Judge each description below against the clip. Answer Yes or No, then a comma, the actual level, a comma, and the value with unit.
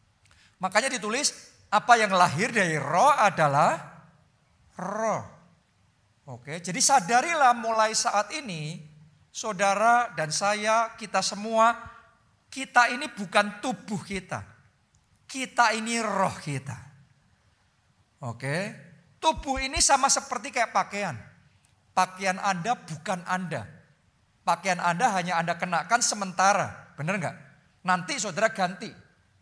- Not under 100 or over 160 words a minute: Yes, average, 105 wpm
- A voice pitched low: No, high, 190 Hz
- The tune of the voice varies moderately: No, wide, 7.1 semitones